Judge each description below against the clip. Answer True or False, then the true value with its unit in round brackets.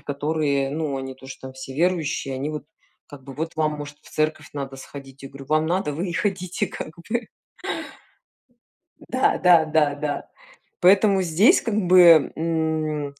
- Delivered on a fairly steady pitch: False (3.5 semitones)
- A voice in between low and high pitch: True (155 Hz)